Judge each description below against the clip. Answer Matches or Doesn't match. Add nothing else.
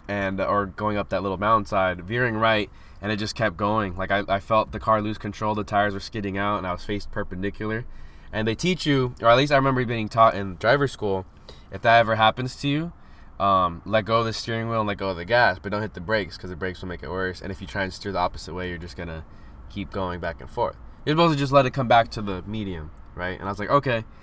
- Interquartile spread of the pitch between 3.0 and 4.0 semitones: Matches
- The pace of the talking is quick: Matches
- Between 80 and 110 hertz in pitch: Matches